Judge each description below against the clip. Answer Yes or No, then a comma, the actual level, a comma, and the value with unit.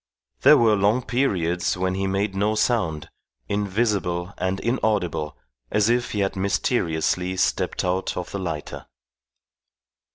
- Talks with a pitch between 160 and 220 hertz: No, very low, 95 Hz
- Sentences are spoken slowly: Yes, slow, 130 wpm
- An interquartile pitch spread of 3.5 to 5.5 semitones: No, average, 3.0 semitones